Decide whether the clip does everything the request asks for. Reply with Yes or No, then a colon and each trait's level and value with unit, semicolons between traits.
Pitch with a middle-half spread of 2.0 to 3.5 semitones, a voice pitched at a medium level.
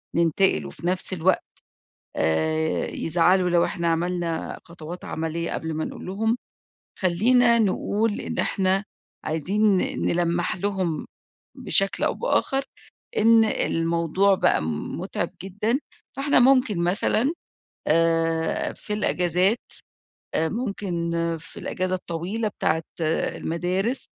No: average, 3.9 semitones; medium, 180 Hz